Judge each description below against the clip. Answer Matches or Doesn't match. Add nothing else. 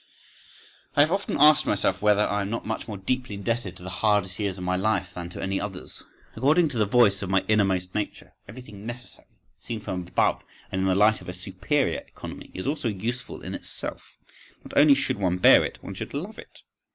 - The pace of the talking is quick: Matches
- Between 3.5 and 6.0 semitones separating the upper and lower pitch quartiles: Matches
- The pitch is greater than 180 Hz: Doesn't match